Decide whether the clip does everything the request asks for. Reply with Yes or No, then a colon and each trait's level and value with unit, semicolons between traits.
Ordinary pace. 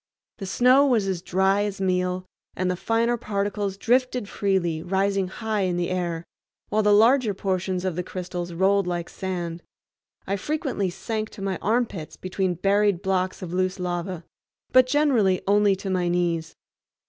Yes: average, 160 wpm